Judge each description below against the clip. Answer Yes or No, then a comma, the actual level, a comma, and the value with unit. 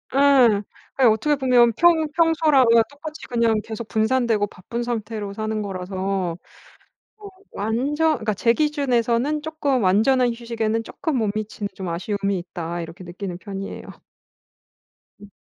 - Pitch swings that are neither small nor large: Yes, average, 5.0 semitones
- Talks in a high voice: Yes, high, 230 Hz